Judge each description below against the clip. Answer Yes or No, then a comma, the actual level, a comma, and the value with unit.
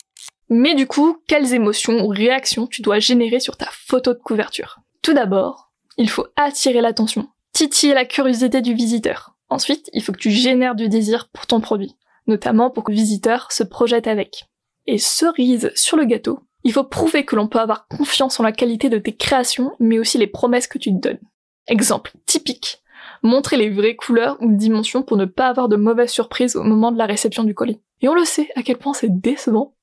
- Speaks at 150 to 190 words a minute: No, average, 205 wpm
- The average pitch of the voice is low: No, high, 240 Hz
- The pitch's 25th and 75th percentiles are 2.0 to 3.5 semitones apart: Yes, average, 3.2 semitones